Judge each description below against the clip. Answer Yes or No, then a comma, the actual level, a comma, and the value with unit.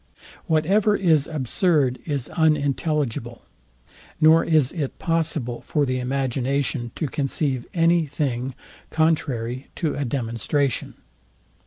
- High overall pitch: No, medium, 145 Hz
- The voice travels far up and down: No, average, 3.8 semitones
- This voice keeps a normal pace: No, slow, 105 wpm